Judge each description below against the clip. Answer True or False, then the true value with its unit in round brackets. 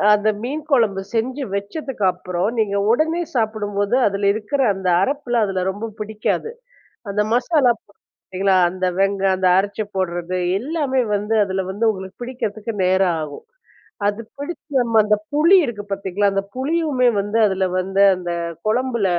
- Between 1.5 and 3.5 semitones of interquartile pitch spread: False (4.5 semitones)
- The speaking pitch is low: False (210 Hz)